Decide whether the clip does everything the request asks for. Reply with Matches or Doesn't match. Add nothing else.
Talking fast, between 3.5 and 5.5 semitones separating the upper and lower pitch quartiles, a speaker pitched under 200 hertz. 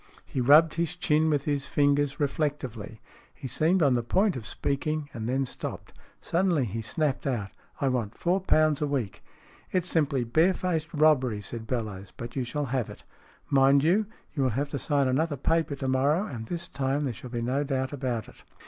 Matches